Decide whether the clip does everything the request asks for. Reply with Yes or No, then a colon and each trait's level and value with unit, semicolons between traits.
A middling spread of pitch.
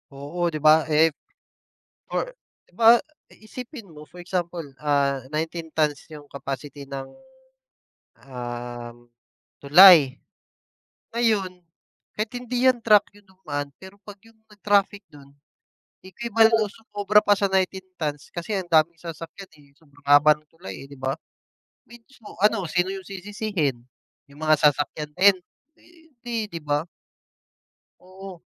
No: wide, 5.7 semitones